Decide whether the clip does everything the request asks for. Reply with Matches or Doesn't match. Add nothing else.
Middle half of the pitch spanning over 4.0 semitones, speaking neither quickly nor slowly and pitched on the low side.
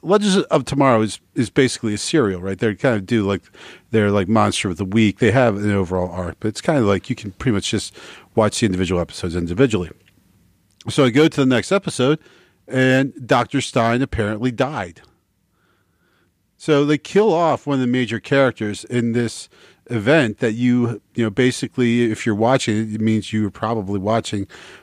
Matches